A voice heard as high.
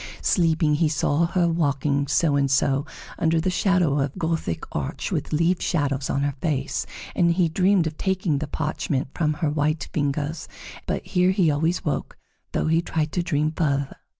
No: medium, 155 Hz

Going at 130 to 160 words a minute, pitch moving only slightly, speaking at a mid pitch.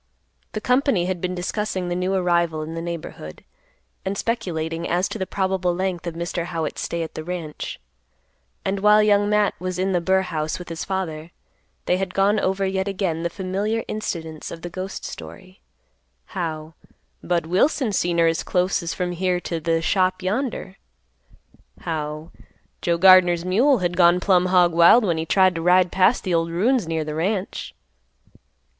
No: average, 175 wpm; narrow, 2.3 semitones; medium, 180 Hz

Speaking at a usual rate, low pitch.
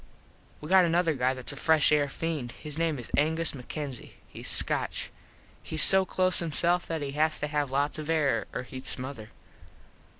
No: average, 180 wpm; medium, 150 Hz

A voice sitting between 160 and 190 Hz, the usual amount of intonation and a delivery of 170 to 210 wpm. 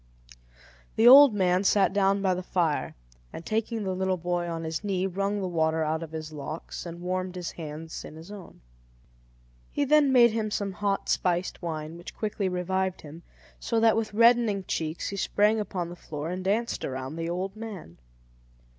Yes: medium, 185 Hz; average, 3.8 semitones; average, 185 wpm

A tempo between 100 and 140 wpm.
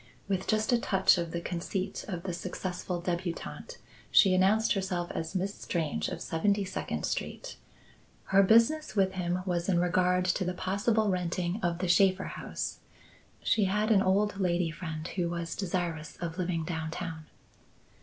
No: average, 160 wpm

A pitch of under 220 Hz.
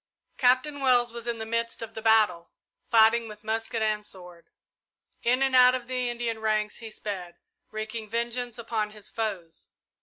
No: high, 225 Hz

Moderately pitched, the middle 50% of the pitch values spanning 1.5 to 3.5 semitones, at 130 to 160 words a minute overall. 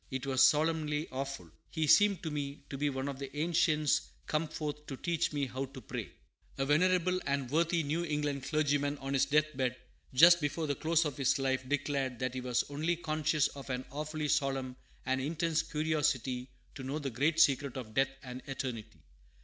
No: medium, 145 Hz; average, 2.7 semitones; average, 190 wpm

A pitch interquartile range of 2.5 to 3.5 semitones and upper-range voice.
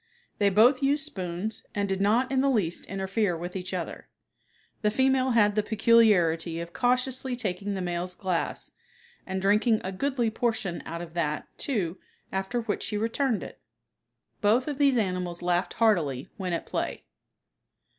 No: average, 4.9 semitones; high, 205 Hz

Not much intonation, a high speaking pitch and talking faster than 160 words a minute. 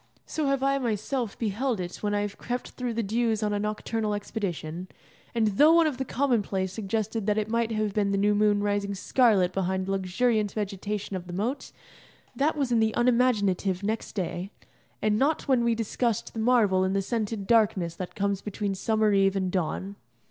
No: average, 3.2 semitones; high, 210 Hz; average, 195 wpm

